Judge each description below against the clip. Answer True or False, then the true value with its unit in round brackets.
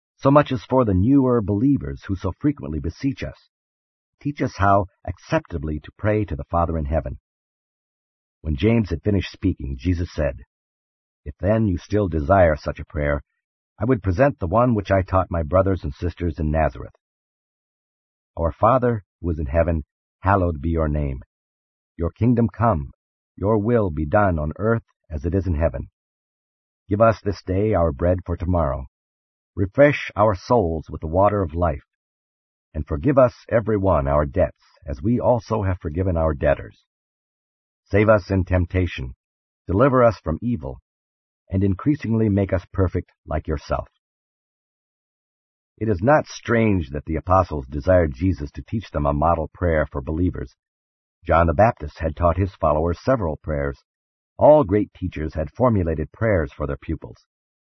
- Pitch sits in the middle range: False (90 Hz)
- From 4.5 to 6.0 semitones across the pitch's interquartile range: True (5.6 semitones)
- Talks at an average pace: True (160 wpm)